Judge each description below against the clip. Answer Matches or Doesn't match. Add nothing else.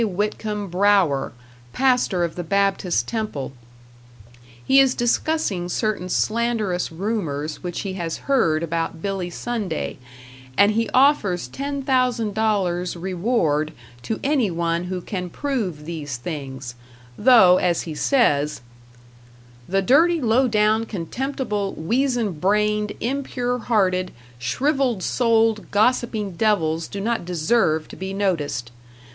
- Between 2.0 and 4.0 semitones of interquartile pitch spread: Doesn't match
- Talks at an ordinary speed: Doesn't match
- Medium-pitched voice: Doesn't match